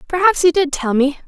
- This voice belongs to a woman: Yes, female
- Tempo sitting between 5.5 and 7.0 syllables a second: Yes, 5.6 syllables/s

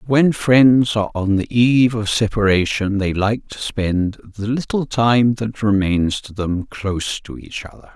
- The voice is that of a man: Yes, male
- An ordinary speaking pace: Yes, average, 180 wpm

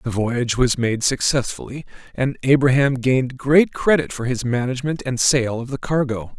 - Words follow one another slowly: No, average, 170 wpm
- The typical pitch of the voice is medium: No, low, 130 Hz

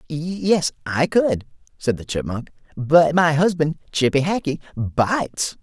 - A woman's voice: No, male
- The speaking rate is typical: No, slow, 130 wpm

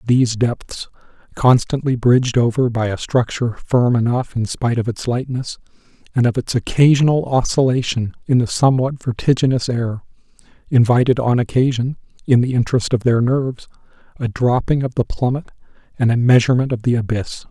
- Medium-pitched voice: No, low, 125 Hz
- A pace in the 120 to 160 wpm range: Yes, average, 155 wpm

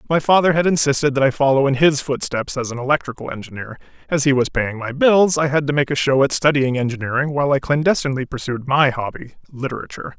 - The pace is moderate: No, fast, 210 wpm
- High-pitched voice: No, medium, 140 Hz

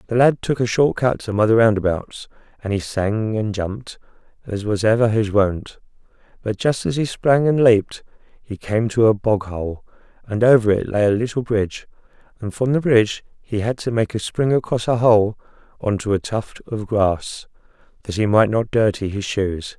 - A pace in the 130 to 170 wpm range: No, average, 195 wpm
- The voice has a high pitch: No, low, 110 Hz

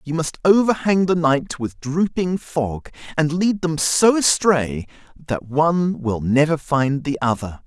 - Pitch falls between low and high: Yes, medium, 155 Hz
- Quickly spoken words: No, average, 155 wpm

